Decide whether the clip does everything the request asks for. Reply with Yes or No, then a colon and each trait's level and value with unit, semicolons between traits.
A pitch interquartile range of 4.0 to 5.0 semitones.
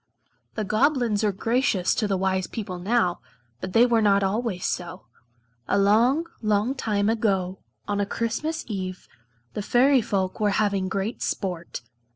No: average, 3.3 semitones